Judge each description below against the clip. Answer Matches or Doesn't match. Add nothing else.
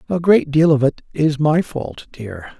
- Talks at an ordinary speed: Doesn't match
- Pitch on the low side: Doesn't match